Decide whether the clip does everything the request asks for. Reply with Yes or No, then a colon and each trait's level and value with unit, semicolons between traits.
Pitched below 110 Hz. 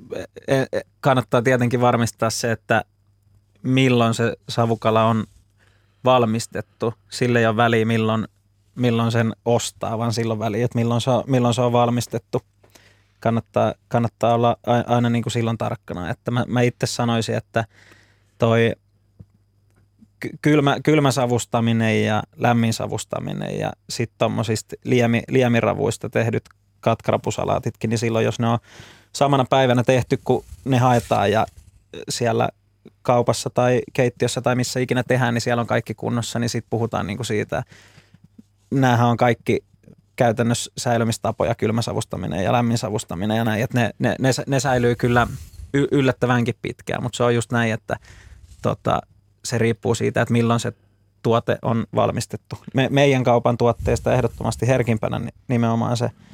No: low, 115 Hz